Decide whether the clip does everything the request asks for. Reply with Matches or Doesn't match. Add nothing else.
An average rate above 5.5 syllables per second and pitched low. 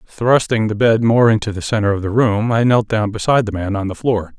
Matches